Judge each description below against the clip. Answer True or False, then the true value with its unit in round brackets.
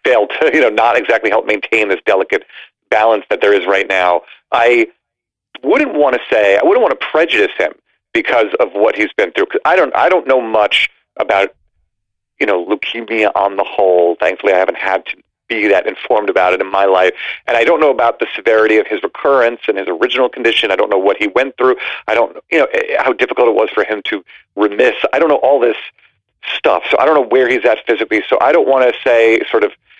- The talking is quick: True (230 wpm)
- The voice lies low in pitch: True (125 Hz)